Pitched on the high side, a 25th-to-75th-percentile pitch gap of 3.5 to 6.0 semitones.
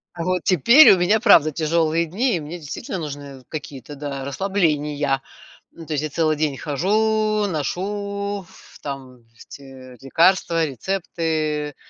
No: medium, 160 Hz; average, 4.9 semitones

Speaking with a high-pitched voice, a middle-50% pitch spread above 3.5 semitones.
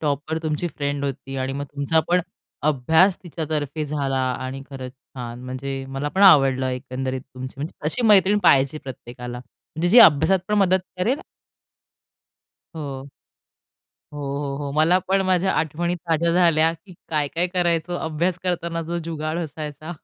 No: medium, 155 Hz; average, 4.1 semitones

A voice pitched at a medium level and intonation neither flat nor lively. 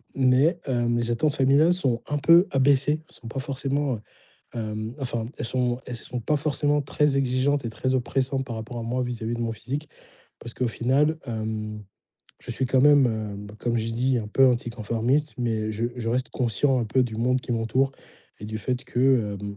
No: low, 125 Hz; average, 3.0 semitones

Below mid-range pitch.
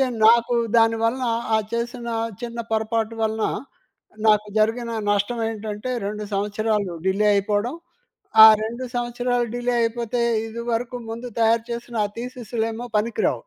No: high, 230 Hz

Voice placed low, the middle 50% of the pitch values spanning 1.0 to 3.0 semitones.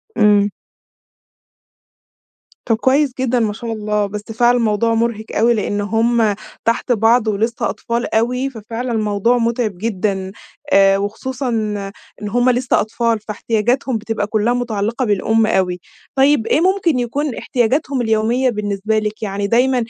No: high, 225 Hz; narrow, 2.6 semitones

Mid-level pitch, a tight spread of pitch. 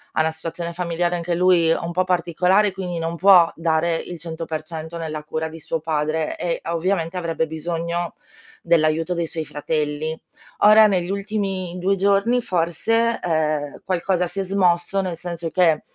Yes: medium, 170 Hz; narrow, 2.3 semitones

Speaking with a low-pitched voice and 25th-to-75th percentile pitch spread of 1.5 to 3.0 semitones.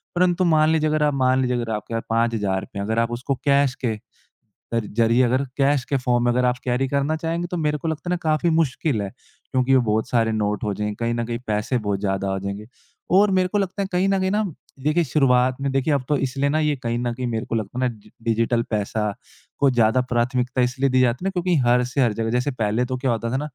No: low, 125 Hz; average, 4.3 semitones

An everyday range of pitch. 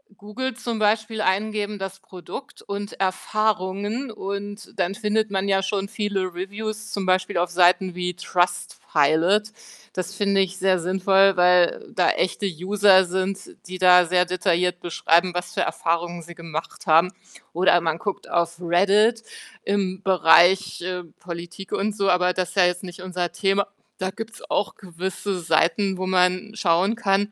No: narrow, 2.3 semitones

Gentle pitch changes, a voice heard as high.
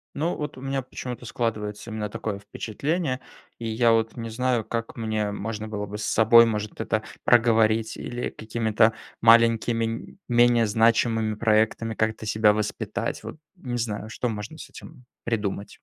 No: narrow, 1.7 semitones; low, 115 Hz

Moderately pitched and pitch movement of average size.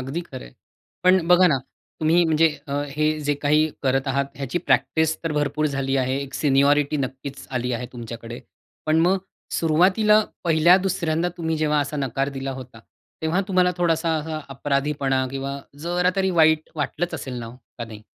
Yes: medium, 150 Hz; average, 3.5 semitones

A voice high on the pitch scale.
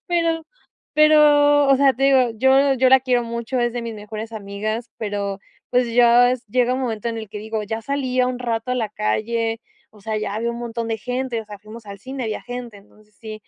Yes: high, 235 Hz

